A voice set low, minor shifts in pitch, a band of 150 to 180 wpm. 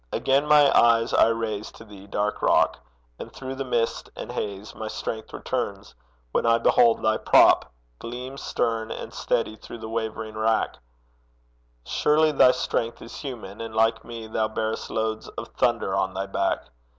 Yes: low, 115 Hz; narrow, 1.5 semitones; average, 165 wpm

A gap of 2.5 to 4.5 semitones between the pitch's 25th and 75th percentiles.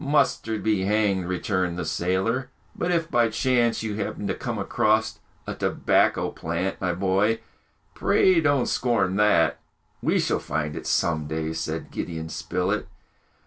No: average, 4.9 semitones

